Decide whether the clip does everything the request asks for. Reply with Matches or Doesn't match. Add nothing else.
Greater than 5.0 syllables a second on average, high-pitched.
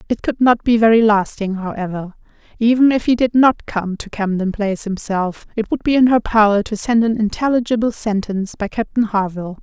Matches